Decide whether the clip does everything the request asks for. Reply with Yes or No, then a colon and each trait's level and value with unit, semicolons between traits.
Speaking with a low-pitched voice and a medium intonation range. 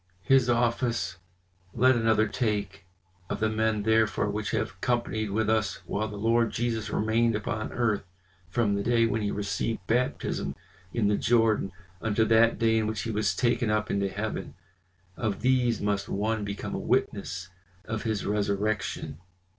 No: low, 110 Hz; narrow, 2.0 semitones